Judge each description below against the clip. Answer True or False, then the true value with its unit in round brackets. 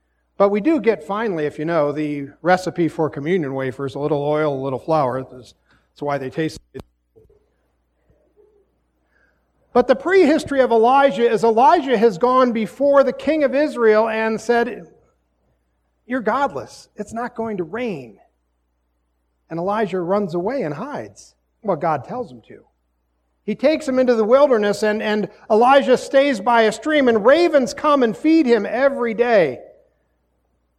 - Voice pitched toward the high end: True (210 Hz)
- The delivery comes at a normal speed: True (155 wpm)